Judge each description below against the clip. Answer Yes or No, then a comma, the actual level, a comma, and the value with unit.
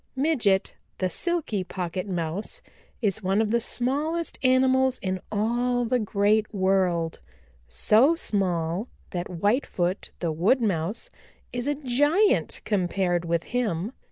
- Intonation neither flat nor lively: No, wide, 5.7 semitones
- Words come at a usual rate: No, slow, 125 wpm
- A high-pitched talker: Yes, high, 210 Hz